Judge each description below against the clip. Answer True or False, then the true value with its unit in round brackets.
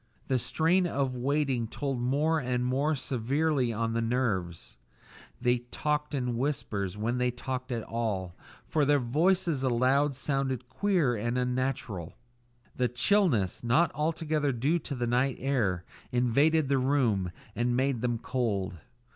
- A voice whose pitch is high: False (125 Hz)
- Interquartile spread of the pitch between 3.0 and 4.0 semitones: True (3.4 semitones)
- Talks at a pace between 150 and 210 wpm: False (140 wpm)